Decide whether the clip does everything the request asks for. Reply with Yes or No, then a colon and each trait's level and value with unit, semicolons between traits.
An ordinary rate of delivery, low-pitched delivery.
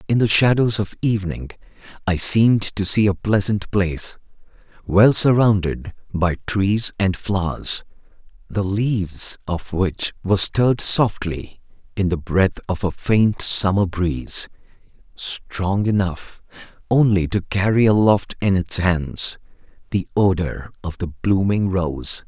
No: slow, 130 wpm; very low, 95 Hz